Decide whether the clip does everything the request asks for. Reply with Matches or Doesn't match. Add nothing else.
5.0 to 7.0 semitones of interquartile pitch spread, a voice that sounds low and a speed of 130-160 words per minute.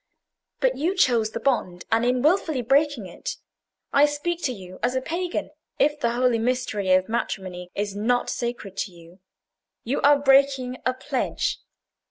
Doesn't match